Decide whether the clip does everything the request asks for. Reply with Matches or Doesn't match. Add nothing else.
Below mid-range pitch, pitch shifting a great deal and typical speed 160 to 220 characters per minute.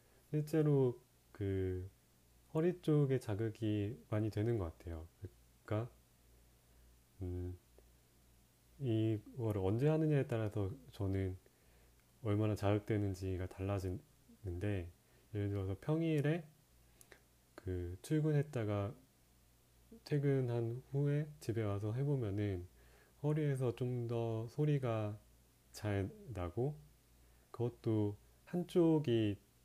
Matches